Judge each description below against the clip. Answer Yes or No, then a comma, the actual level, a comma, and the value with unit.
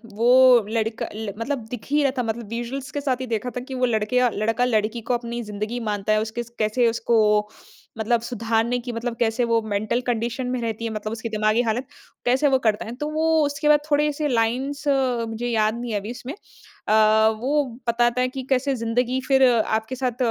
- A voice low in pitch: No, high, 235 Hz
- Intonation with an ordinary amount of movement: No, narrow, 2.3 semitones